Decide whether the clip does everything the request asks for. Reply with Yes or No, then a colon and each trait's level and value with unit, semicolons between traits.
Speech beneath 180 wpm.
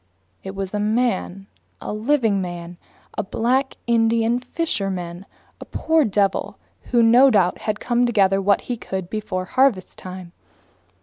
Yes: average, 145 wpm